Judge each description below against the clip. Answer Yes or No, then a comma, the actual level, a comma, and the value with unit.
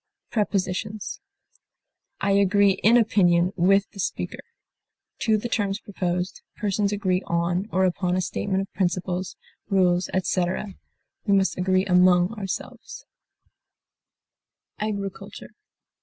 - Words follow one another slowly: Yes, slow, 110 wpm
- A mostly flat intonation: Yes, narrow, 2.0 semitones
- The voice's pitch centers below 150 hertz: No, high, 190 Hz